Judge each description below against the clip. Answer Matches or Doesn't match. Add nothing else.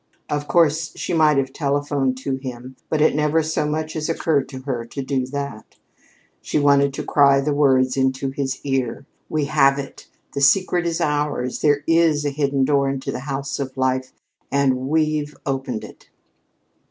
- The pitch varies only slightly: Matches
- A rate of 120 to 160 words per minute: Doesn't match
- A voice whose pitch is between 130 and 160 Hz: Matches